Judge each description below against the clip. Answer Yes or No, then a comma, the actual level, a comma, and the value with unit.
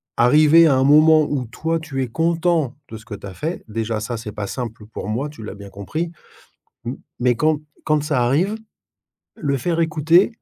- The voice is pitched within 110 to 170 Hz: Yes, medium, 140 Hz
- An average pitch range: No, wide, 5.8 semitones